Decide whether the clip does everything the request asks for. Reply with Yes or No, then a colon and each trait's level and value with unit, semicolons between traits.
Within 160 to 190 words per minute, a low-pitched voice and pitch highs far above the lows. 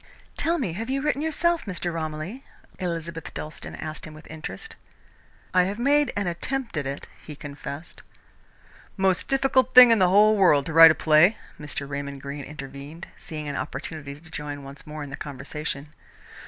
No: average, 175 wpm; medium, 160 Hz; wide, 6.3 semitones